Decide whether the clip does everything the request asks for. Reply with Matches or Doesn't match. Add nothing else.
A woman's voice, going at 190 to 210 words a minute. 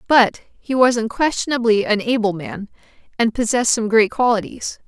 Doesn't match